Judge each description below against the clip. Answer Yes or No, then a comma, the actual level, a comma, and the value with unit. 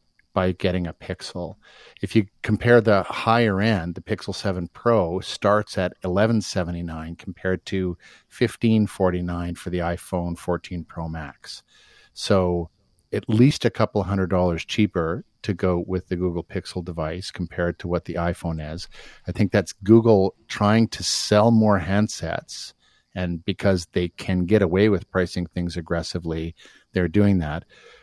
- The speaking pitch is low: Yes, very low, 95 Hz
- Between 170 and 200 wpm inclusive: No, average, 150 wpm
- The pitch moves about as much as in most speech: Yes, average, 3.2 semitones